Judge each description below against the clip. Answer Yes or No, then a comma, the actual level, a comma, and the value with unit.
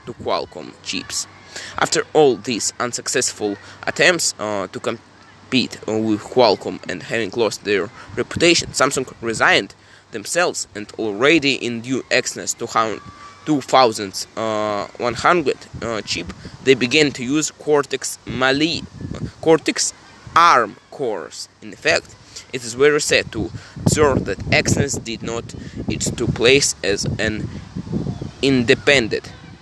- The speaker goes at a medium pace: No, slow, 120 wpm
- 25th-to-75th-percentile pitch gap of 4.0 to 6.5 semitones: Yes, average, 5.0 semitones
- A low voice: Yes, low, 125 Hz